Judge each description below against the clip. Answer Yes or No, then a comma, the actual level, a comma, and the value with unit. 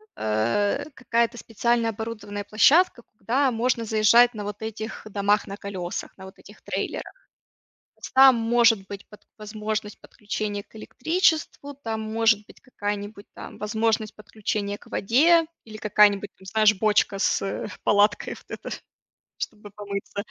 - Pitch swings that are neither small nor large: No, narrow, 2.2 semitones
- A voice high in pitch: Yes, high, 215 Hz